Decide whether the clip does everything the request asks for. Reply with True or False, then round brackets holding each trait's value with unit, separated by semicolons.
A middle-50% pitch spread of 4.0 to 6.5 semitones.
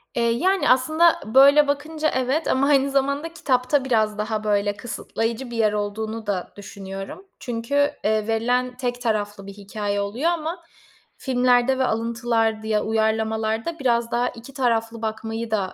False (3.5 semitones)